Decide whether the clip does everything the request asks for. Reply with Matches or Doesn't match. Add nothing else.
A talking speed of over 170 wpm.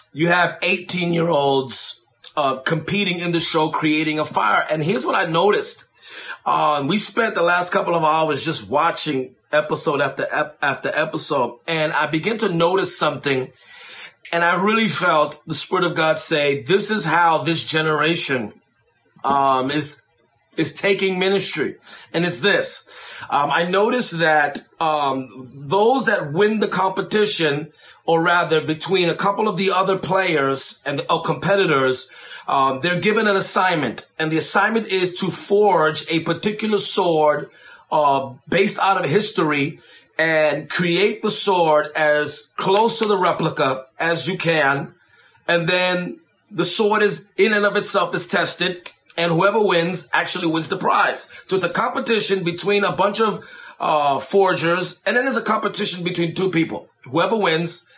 Doesn't match